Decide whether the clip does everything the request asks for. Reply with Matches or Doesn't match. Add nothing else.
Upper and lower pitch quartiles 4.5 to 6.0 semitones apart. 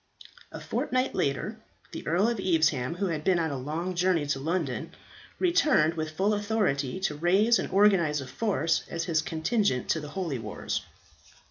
Matches